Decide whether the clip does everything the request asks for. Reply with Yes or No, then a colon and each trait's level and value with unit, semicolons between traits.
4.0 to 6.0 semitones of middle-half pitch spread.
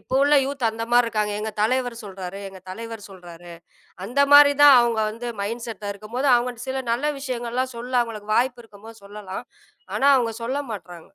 No: average, 3.4 semitones